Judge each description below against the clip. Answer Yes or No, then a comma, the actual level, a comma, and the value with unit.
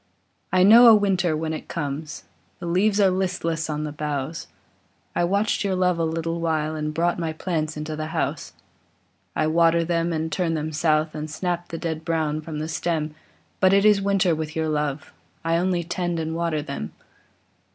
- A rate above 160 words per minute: Yes, average, 190 wpm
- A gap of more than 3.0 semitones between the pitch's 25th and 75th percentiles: No, narrow, 2.4 semitones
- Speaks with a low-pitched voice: No, medium, 165 Hz